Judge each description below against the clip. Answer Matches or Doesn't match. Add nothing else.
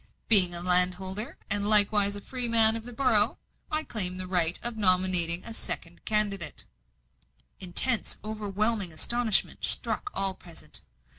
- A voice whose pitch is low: Doesn't match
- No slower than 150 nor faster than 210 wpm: Doesn't match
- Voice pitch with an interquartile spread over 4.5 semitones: Doesn't match